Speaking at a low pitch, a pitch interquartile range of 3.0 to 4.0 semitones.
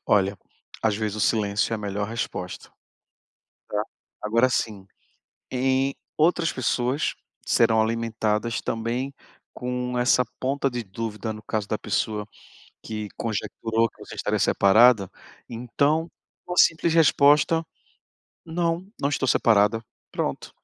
Yes: low, 115 Hz; average, 3.7 semitones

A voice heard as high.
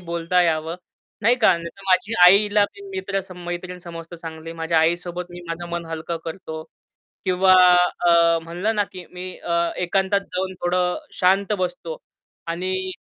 No: medium, 180 Hz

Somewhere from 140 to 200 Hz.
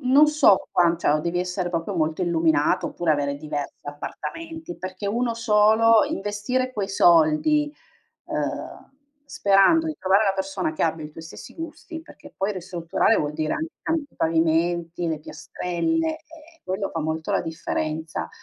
Yes: high, 190 Hz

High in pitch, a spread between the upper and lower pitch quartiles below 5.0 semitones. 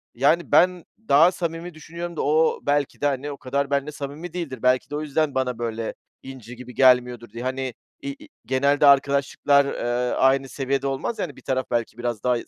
No: medium, 140 Hz; average, 2.9 semitones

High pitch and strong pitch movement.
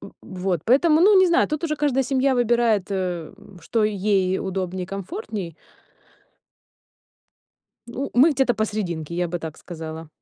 Yes: high, 205 Hz; wide, 6.9 semitones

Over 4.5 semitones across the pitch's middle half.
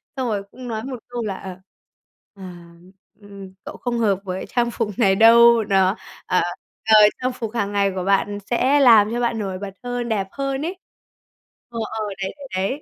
No: average, 3.6 semitones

